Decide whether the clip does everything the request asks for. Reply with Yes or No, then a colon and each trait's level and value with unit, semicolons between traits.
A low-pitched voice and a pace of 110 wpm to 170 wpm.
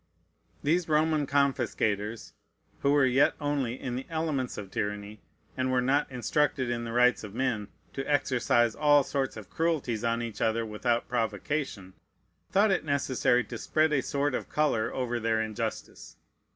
Yes: low, 125 Hz; average, 160 wpm